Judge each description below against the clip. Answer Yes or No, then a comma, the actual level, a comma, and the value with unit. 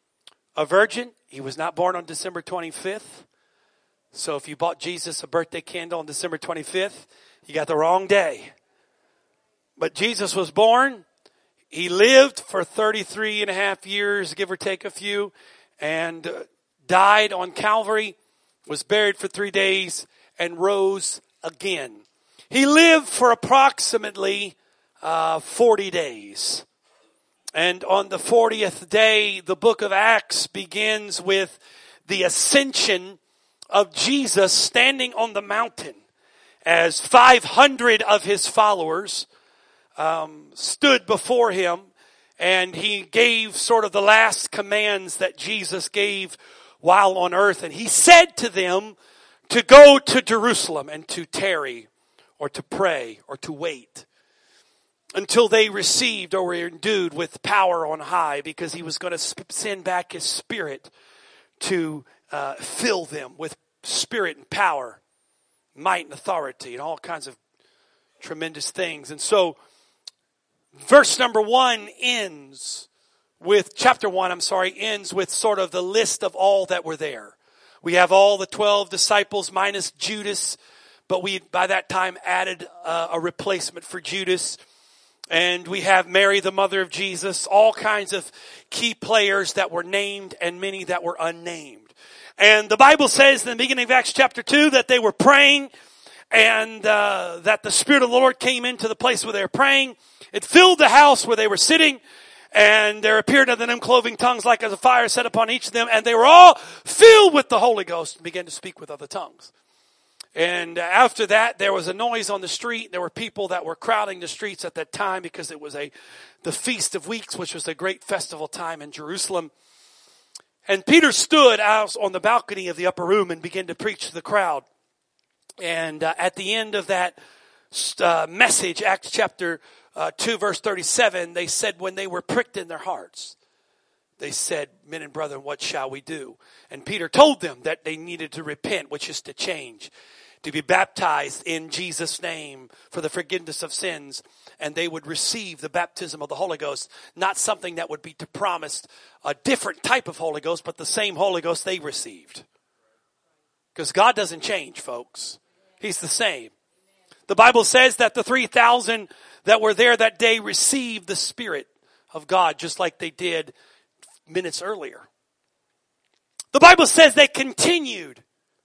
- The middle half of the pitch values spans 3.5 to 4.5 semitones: No, average, 5.2 semitones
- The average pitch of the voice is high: Yes, high, 200 Hz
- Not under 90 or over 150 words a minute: No, average, 165 wpm